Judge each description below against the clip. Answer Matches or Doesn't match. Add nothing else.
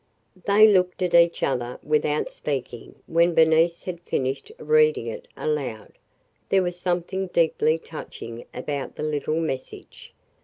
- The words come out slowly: Matches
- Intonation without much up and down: Doesn't match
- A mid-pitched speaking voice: Matches